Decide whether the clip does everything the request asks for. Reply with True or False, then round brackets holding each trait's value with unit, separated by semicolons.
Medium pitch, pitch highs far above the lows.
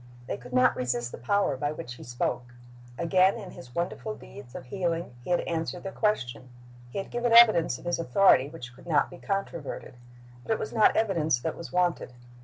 True (165 Hz; 7.5 semitones)